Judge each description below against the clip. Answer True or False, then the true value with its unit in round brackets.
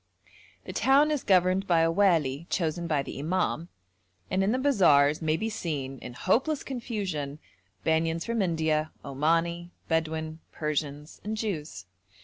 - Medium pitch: True (165 Hz)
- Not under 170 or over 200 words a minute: False (140 wpm)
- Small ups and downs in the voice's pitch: False (4.3 semitones)